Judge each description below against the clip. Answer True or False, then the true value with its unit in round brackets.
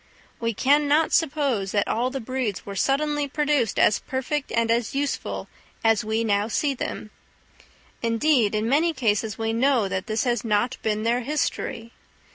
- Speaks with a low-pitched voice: False (235 Hz)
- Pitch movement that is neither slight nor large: True (4.4 semitones)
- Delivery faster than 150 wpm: True (165 wpm)